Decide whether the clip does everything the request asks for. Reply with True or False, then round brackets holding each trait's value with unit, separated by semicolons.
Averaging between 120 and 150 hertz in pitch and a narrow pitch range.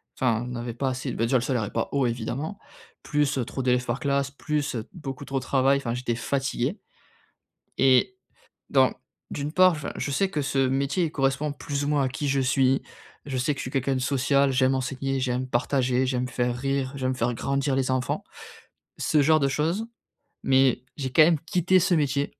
True (135 Hz; 2.0 semitones)